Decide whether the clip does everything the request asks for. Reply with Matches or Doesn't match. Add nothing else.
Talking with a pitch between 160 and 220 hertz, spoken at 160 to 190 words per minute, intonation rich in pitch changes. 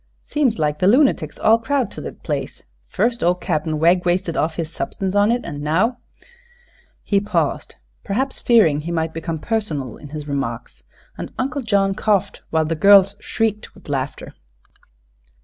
Matches